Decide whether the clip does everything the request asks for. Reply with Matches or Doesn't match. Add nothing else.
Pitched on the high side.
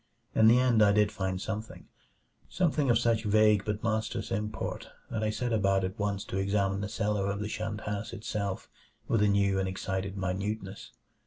Doesn't match